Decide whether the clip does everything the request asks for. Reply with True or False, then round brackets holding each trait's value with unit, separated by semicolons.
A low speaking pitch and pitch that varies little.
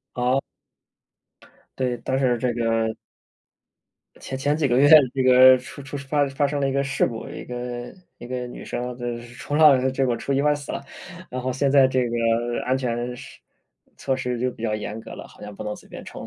True (130 Hz; 1.9 semitones)